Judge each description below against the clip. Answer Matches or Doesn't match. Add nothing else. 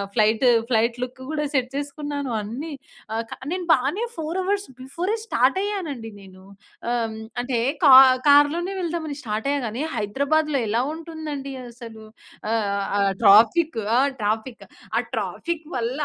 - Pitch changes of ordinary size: Doesn't match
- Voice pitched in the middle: Doesn't match